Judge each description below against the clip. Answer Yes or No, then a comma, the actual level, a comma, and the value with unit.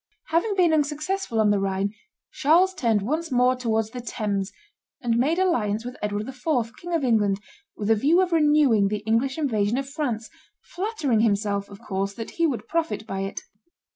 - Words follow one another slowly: No, average, 180 wpm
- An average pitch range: No, wide, 6.7 semitones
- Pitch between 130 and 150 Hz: No, high, 245 Hz